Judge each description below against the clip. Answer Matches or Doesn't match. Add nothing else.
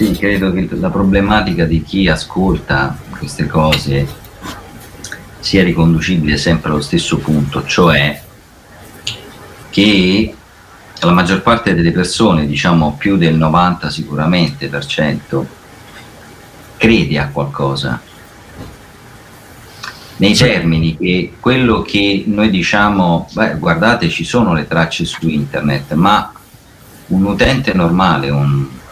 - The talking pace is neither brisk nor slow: Doesn't match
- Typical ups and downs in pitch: Matches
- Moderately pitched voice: Doesn't match